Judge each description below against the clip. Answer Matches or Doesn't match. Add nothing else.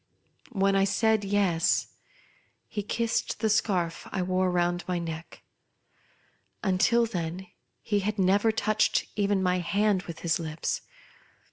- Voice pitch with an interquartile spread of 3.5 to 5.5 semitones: Doesn't match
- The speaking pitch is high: Matches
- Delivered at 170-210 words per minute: Doesn't match